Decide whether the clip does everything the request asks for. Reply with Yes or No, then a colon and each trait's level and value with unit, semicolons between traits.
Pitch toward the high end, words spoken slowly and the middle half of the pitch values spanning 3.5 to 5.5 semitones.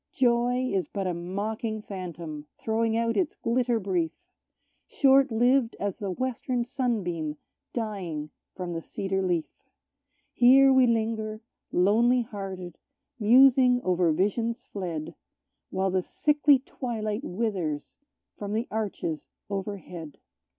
Yes: high, 215 Hz; slow, 115 wpm; average, 4.9 semitones